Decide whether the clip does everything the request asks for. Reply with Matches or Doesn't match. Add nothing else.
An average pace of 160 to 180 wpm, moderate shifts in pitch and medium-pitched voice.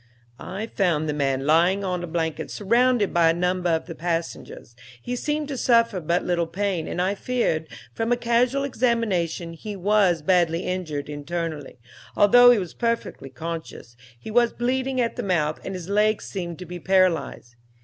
Doesn't match